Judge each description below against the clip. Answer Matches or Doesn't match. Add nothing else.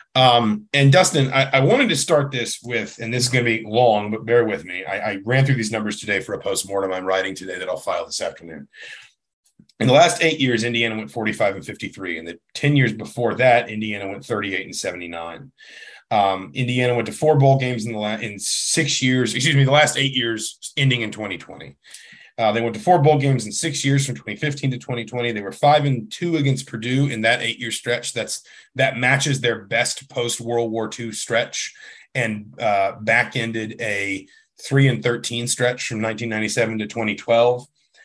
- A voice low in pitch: Matches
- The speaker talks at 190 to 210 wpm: Matches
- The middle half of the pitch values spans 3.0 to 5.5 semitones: Matches